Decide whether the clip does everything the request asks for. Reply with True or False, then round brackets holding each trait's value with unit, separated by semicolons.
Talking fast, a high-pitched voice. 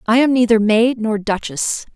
False (185 wpm; 225 Hz)